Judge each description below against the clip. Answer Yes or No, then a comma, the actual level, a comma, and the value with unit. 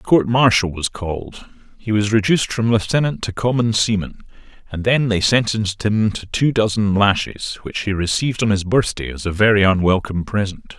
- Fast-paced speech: No, average, 185 wpm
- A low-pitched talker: Yes, low, 105 Hz